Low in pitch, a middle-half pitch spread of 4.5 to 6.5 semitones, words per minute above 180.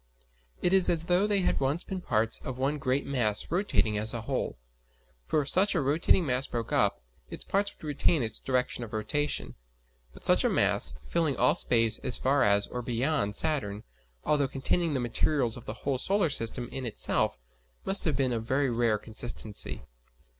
Yes: low, 130 Hz; average, 5.1 semitones; average, 190 wpm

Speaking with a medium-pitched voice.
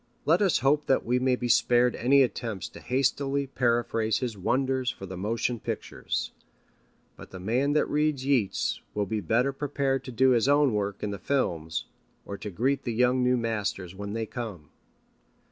No: low, 125 Hz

